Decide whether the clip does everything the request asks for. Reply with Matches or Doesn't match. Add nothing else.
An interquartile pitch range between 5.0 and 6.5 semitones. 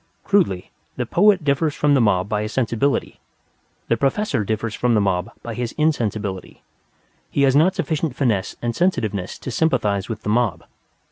Matches